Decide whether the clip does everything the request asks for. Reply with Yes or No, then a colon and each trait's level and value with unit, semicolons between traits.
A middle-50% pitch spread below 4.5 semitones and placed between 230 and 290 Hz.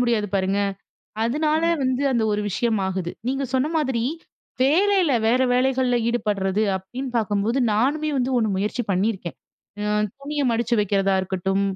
No: average, 4.9 semitones; high, 235 Hz